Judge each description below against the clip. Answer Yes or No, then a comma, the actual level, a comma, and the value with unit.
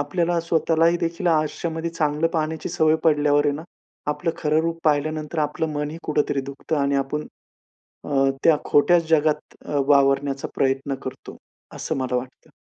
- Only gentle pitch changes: Yes, narrow, 2.2 semitones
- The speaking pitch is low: No, medium, 150 Hz